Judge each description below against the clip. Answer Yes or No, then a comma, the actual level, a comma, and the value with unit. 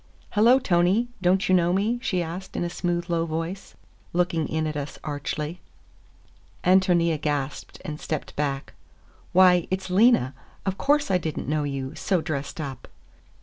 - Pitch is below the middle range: No, medium, 175 Hz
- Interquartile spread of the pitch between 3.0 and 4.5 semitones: Yes, average, 3.6 semitones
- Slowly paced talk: No, average, 160 wpm